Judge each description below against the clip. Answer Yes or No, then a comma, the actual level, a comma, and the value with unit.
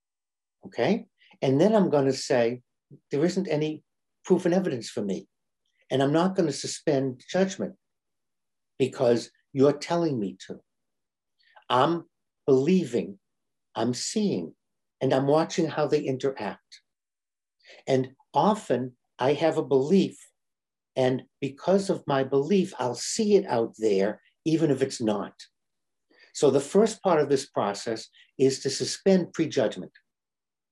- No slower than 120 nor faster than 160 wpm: Yes, slow, 135 wpm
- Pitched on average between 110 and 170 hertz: Yes, medium, 140 Hz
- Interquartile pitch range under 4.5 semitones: No, average, 5.1 semitones